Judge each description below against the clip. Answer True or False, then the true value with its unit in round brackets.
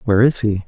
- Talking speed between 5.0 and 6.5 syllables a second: False (7.3 syllables/s)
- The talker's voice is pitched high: False (105 Hz)